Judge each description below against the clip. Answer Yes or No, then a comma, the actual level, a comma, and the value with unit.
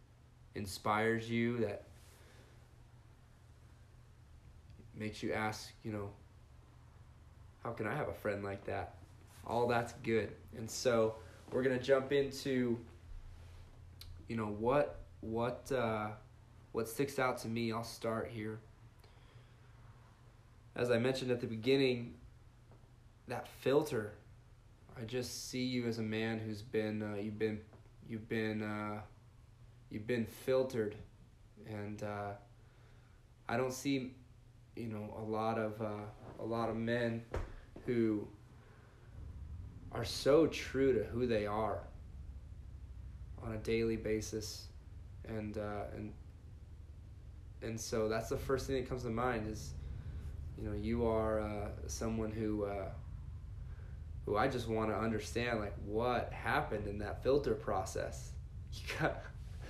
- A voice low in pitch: Yes, low, 110 Hz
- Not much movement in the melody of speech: Yes, narrow, 2.1 semitones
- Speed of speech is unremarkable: No, slow, 130 wpm